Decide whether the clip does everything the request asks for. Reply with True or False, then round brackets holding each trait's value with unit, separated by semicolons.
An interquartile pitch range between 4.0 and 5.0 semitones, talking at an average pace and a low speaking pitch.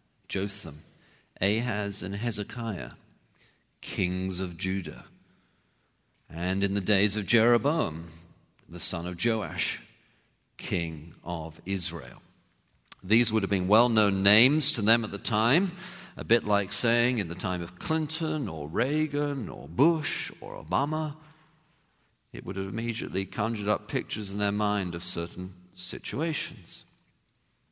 False (4.6 semitones; 130 wpm; 105 Hz)